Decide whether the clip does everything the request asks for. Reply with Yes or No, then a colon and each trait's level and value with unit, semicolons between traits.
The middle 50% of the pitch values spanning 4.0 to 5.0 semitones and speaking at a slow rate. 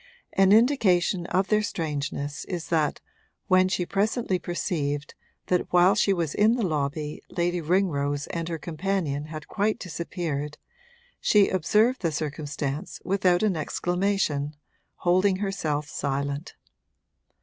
Yes: average, 4.5 semitones; slow, 125 wpm